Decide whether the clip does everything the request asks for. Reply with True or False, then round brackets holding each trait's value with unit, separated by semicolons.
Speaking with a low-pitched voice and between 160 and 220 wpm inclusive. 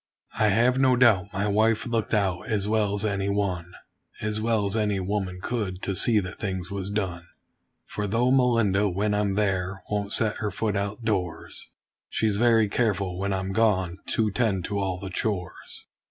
True (100 Hz; 180 wpm)